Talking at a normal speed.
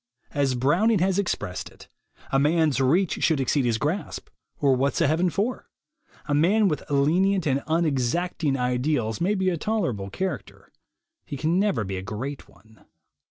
Yes: average, 160 wpm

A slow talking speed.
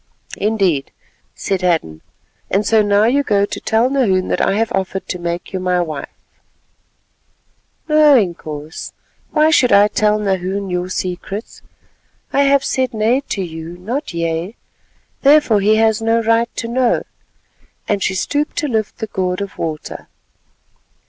No: average, 150 wpm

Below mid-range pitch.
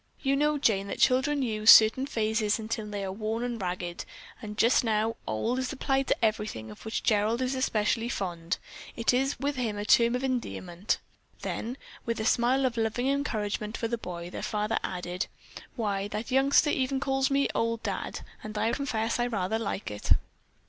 No: high, 225 Hz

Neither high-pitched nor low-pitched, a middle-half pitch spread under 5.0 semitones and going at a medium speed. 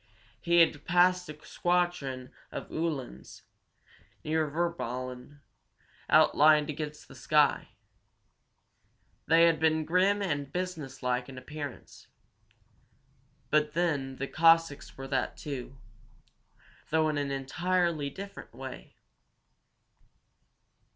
No: medium, 150 Hz; average, 3.7 semitones; slow, 100 wpm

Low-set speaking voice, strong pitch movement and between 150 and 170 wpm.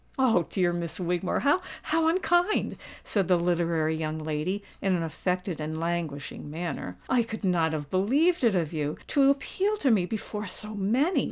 No: medium, 180 Hz; wide, 6.7 semitones; average, 165 wpm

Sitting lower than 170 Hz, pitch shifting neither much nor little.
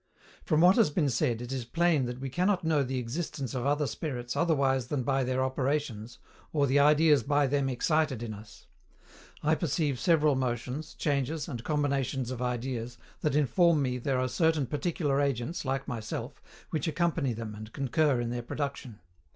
Yes: low, 135 Hz; average, 3.5 semitones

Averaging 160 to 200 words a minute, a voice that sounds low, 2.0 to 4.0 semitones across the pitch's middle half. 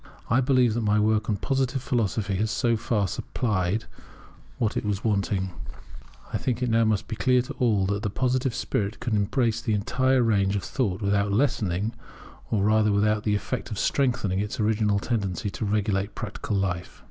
Yes: average, 180 wpm; low, 105 Hz; average, 2.8 semitones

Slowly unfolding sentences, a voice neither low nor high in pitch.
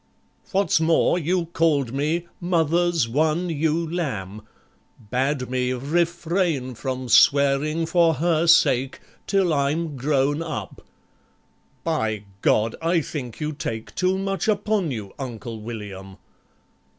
Yes: slow, 115 wpm; medium, 150 Hz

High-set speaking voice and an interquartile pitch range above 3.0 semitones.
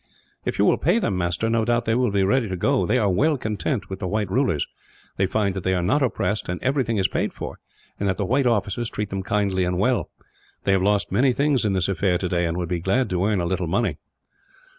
No: low, 100 Hz; average, 4.3 semitones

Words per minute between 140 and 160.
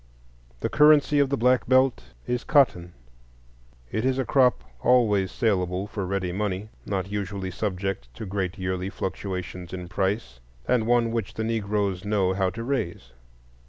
Yes: average, 155 wpm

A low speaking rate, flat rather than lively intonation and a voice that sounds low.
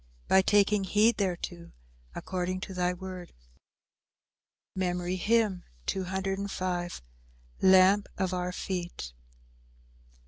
No: slow, 80 wpm; narrow, 1.5 semitones; medium, 185 Hz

